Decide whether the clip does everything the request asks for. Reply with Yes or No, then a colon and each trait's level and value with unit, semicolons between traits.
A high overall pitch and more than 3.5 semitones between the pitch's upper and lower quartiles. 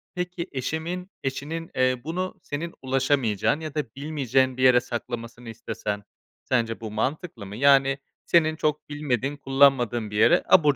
No: low, 135 Hz; average, 4.2 semitones